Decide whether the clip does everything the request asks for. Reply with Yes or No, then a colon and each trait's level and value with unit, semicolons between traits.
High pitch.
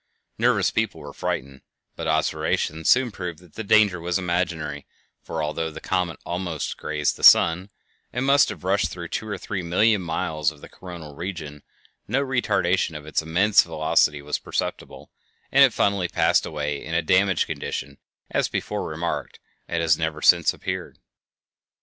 No: very low, 85 Hz